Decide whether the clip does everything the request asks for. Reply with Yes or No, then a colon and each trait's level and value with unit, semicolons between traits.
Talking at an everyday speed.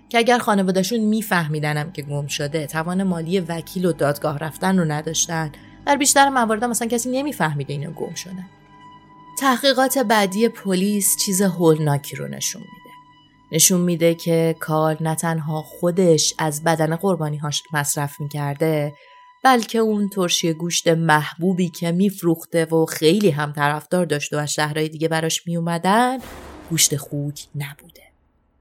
Yes: average, 145 wpm